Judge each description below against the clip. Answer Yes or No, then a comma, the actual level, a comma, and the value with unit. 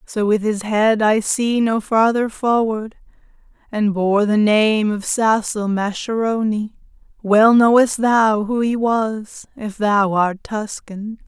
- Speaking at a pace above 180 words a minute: No, average, 140 wpm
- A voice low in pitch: No, high, 215 Hz